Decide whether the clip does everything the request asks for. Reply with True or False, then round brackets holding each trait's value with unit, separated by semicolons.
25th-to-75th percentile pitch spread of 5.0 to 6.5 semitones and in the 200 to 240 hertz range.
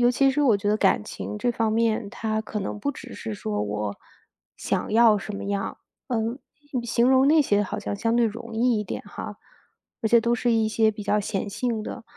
False (2.4 semitones; 220 Hz)